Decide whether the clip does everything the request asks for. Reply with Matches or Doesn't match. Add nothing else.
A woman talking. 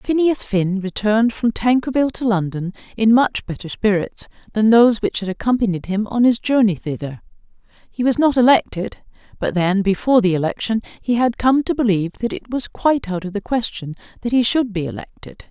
Matches